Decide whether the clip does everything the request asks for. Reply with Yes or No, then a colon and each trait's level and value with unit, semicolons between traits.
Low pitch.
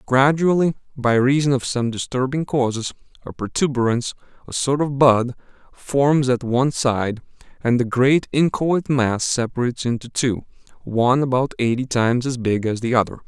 Yes: low, 130 Hz